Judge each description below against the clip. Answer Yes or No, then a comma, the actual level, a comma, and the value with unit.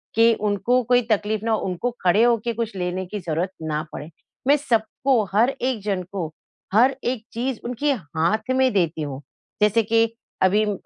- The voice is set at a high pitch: Yes, high, 215 Hz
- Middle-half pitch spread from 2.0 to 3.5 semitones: No, average, 4.5 semitones